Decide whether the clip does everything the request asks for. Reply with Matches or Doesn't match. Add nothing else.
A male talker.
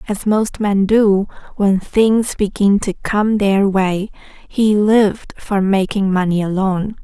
Doesn't match